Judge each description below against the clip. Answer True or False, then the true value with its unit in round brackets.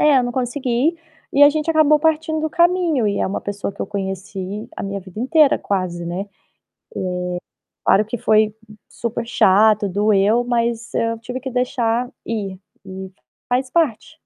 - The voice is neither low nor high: False (230 Hz)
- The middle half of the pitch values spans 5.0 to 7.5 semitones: True (5.4 semitones)